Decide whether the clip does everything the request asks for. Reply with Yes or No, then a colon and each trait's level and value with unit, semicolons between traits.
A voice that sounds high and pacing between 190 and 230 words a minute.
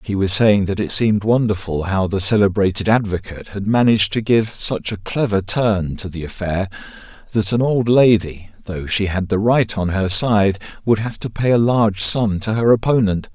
No: low, 105 Hz; average, 200 wpm